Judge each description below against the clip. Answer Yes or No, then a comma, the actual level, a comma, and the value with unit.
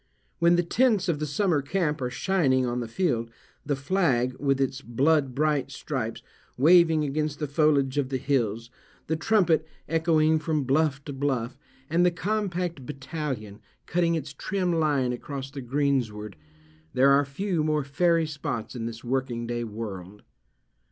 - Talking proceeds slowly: No, average, 150 wpm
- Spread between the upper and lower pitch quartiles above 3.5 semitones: Yes, average, 4.4 semitones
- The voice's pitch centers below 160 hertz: Yes, medium, 140 Hz